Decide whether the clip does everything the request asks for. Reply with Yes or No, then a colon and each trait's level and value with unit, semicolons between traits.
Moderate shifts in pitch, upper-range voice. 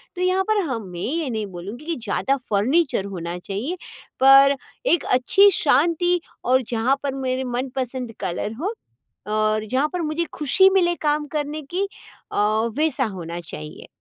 No: wide, 7.1 semitones; very high, 265 Hz